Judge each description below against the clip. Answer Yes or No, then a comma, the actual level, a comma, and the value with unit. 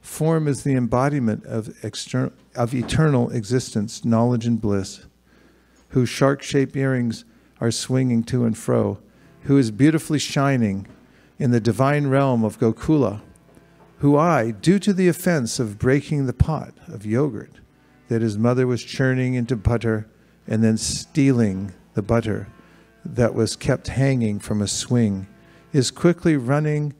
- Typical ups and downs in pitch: Yes, average, 3.7 semitones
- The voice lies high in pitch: No, low, 125 Hz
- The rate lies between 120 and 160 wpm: Yes, average, 145 wpm